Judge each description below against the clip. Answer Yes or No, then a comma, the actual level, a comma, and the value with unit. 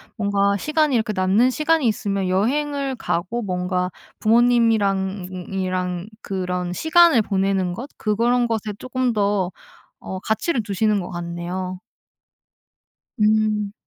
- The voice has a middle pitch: No, high, 205 Hz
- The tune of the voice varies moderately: Yes, average, 4.3 semitones